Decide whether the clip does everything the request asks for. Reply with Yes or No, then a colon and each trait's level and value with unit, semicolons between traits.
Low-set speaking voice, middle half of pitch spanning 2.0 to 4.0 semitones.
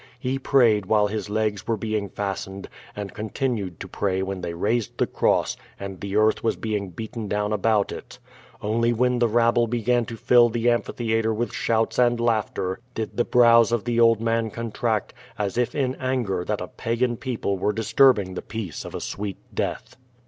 Yes: low, 110 Hz; narrow, 2.5 semitones